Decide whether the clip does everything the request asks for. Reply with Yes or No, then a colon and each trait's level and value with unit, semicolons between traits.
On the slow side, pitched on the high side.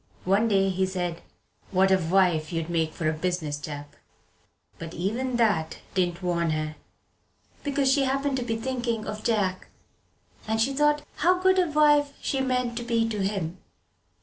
No: average, 170 wpm; high, 205 Hz